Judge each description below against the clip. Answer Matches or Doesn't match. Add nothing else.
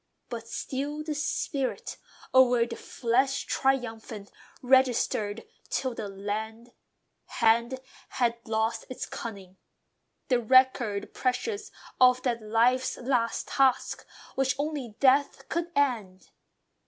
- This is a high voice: Matches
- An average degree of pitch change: Matches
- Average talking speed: Doesn't match